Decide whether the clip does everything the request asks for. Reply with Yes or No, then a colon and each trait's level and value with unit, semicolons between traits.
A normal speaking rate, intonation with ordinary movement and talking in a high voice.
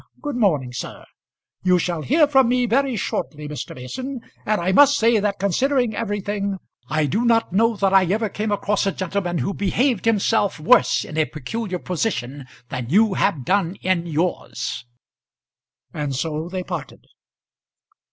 No: average, 160 wpm; wide, 5.8 semitones; high, 195 Hz